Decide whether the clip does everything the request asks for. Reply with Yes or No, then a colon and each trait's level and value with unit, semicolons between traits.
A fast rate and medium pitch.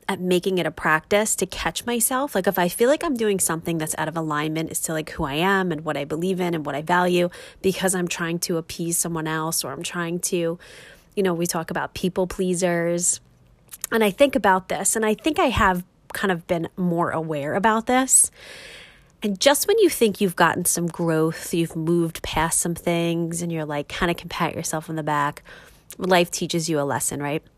Yes: fast, 220 wpm; medium, 175 Hz